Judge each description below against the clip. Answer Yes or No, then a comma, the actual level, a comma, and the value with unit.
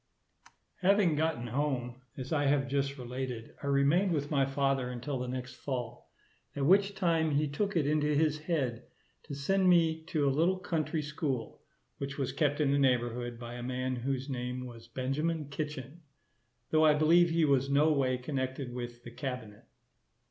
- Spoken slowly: No, average, 175 wpm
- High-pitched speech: No, medium, 140 Hz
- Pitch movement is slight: No, average, 3.4 semitones